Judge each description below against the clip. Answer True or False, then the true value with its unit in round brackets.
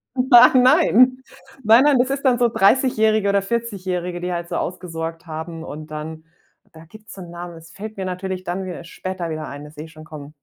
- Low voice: False (180 Hz)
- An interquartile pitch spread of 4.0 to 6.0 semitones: True (5.1 semitones)